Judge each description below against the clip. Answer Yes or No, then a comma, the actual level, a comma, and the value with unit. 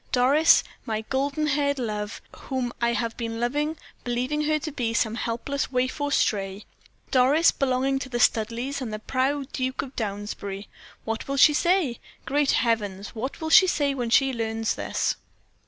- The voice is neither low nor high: No, very high, 255 Hz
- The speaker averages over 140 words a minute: Yes, average, 170 wpm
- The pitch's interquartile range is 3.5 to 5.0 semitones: Yes, average, 3.8 semitones